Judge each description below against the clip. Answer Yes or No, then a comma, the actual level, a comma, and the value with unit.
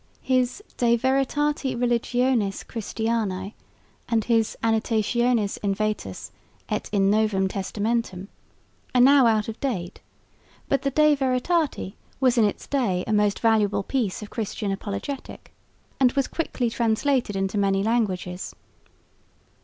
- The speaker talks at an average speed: No, slow, 125 wpm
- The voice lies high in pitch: Yes, high, 225 Hz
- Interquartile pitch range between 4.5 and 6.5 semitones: No, average, 3.9 semitones